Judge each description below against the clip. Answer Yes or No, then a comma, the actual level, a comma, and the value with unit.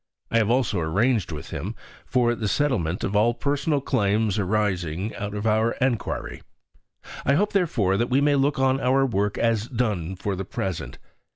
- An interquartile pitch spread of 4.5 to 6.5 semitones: Yes, average, 5.0 semitones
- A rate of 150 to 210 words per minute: Yes, average, 175 wpm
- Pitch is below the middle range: Yes, low, 110 Hz